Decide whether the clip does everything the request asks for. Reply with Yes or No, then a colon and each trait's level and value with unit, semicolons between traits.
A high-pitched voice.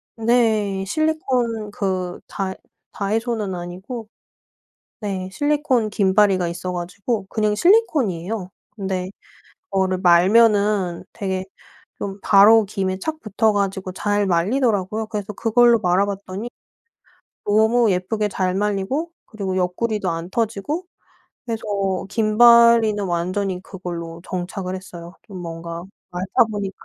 Yes: high, 200 Hz